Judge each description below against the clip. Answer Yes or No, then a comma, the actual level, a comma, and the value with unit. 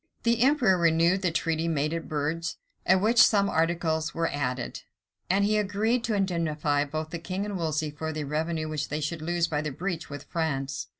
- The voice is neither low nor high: Yes, medium, 165 Hz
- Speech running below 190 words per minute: No, average, 195 wpm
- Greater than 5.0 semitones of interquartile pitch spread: No, average, 3.6 semitones